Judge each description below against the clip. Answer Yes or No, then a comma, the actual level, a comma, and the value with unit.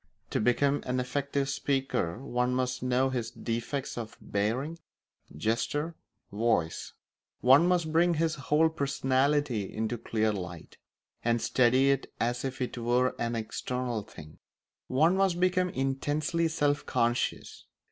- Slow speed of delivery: Yes, slow, 130 wpm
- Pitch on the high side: No, low, 130 Hz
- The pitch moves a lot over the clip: No, average, 3.7 semitones